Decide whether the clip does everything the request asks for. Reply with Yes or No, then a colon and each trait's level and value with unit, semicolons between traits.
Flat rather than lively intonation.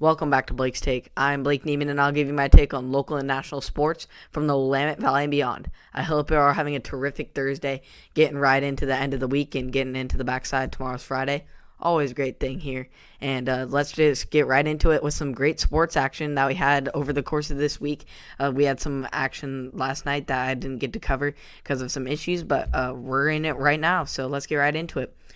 Yes: narrow, 1.7 semitones